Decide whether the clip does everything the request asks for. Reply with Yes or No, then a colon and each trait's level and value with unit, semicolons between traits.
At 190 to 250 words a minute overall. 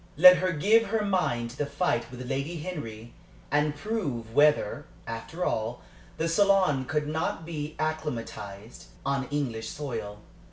No: average, 145 wpm